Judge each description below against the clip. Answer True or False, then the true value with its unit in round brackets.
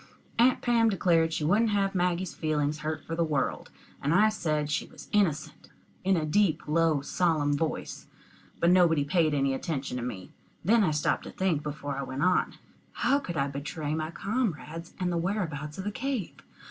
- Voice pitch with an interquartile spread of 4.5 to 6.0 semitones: False (4.1 semitones)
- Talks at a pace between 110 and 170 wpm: False (185 wpm)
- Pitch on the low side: False (165 Hz)